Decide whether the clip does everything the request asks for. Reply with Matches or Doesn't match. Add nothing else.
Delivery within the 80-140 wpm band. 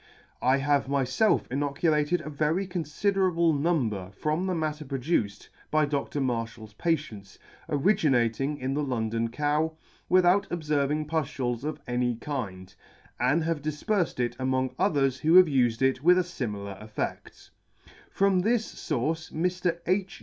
Matches